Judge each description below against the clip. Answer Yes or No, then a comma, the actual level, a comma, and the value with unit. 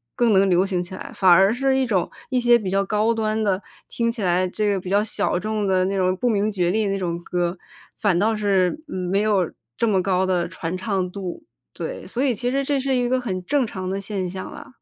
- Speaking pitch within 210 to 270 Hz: No, high, 195 Hz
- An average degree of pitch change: Yes, average, 3.4 semitones